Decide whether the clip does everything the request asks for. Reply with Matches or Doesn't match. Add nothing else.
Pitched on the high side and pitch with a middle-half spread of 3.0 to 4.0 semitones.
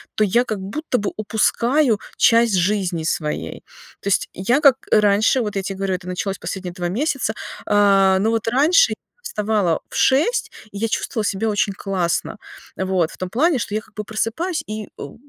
Matches